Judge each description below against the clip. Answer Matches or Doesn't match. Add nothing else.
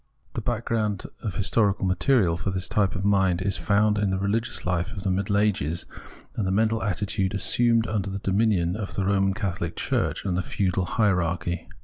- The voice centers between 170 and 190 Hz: Doesn't match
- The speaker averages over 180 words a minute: Matches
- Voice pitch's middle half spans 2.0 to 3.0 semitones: Matches